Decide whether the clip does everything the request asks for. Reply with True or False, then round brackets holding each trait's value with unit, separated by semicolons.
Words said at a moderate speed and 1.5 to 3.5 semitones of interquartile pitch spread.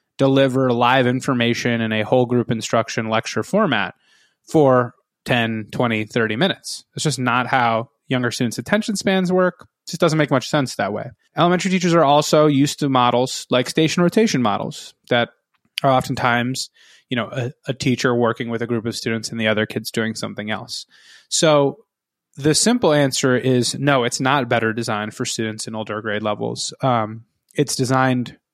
False (175 wpm; 3.9 semitones)